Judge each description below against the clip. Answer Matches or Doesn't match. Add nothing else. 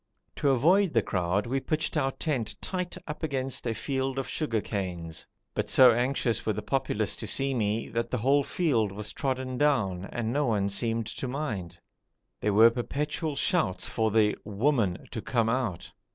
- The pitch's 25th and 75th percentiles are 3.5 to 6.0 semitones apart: Matches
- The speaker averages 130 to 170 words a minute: Doesn't match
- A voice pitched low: Matches